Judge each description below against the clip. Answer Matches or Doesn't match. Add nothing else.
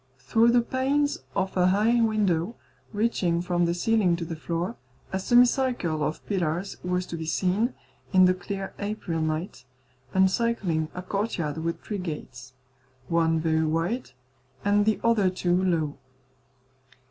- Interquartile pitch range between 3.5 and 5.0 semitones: Matches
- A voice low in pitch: Doesn't match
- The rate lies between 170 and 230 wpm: Doesn't match